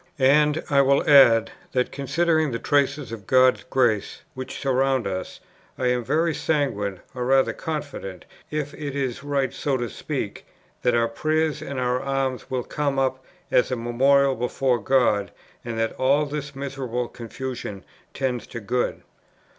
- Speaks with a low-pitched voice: Yes, low, 130 Hz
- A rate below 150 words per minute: No, average, 155 wpm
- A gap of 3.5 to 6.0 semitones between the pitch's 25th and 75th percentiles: No, narrow, 2.6 semitones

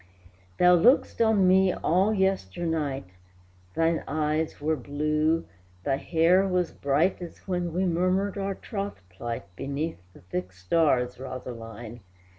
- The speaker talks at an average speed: No, slow, 125 wpm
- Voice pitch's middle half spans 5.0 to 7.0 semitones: Yes, wide, 5.6 semitones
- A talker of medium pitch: Yes, medium, 160 Hz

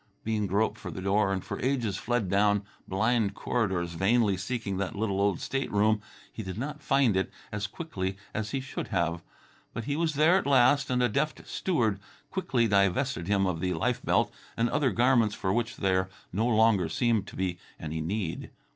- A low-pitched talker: Yes, low, 105 Hz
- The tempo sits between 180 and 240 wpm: Yes, average, 190 wpm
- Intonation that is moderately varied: Yes, average, 4.4 semitones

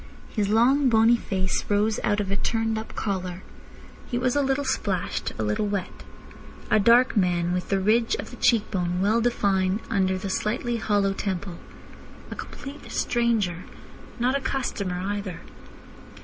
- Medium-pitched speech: No, high, 205 Hz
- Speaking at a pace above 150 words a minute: Yes, average, 160 wpm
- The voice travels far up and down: No, average, 3.9 semitones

